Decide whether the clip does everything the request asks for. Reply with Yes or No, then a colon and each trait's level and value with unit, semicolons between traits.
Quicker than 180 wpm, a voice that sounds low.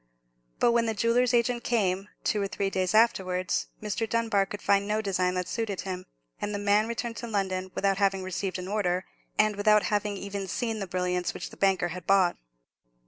No: average, 195 wpm; high, 200 Hz